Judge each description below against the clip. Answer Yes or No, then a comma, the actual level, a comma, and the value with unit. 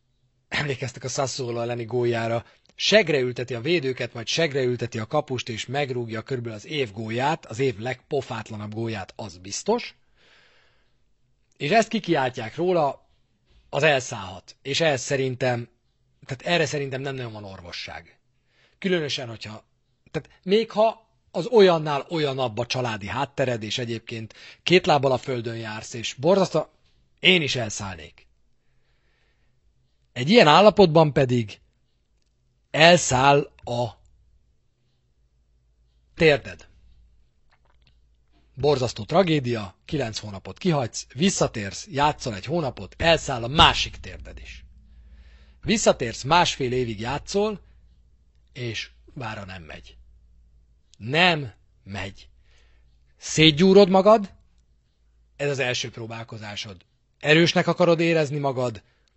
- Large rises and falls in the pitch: Yes, wide, 6.8 semitones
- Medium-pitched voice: No, low, 125 Hz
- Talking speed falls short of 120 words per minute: Yes, slow, 105 wpm